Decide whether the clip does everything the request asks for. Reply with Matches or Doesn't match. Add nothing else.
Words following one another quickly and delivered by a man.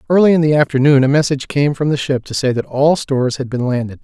Matches